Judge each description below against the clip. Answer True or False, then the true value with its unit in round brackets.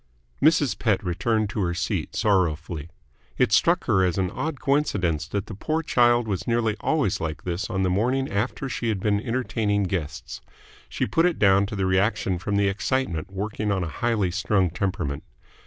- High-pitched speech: False (100 Hz)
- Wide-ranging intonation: False (4.3 semitones)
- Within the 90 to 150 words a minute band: False (185 wpm)